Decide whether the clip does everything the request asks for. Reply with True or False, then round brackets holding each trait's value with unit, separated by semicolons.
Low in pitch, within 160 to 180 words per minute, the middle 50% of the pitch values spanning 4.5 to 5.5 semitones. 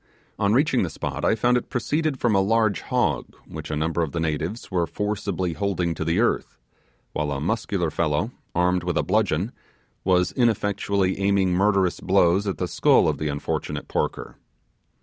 False (95 Hz; 170 wpm; 3.7 semitones)